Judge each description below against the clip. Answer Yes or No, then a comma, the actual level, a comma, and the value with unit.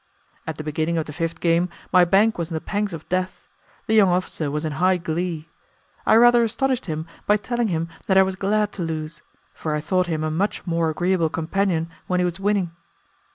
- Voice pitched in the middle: Yes, medium, 175 Hz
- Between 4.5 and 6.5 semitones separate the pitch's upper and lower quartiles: No, average, 3.4 semitones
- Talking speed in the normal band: No, fast, 215 wpm